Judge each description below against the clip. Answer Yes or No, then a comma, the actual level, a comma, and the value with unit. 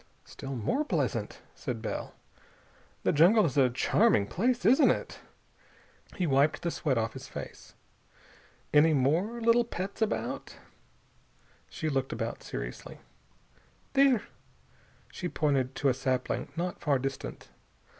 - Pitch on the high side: No, medium, 155 Hz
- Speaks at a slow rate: Yes, slow, 125 wpm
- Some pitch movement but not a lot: No, wide, 7.9 semitones